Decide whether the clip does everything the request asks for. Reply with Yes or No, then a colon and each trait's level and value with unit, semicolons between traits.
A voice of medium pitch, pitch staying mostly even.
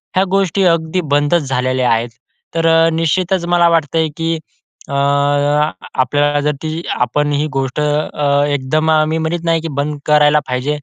Yes: medium, 155 Hz; narrow, 2.3 semitones